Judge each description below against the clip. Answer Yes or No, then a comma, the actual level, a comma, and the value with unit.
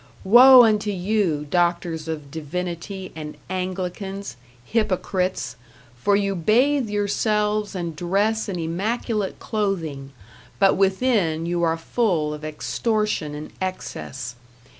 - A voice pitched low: No, medium, 185 Hz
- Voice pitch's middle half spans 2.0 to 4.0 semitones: No, average, 4.5 semitones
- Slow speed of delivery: Yes, slow, 110 wpm